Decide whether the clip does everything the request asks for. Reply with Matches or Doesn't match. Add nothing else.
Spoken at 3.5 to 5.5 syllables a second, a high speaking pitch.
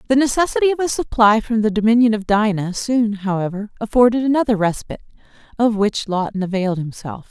Doesn't match